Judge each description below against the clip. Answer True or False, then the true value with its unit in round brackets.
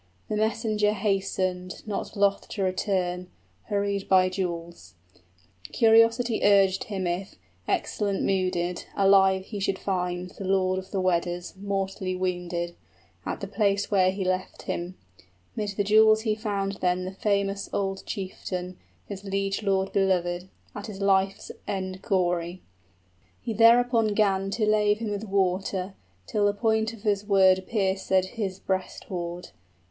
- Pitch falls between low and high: False (195 Hz)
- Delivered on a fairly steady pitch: True (1.8 semitones)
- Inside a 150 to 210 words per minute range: False (140 wpm)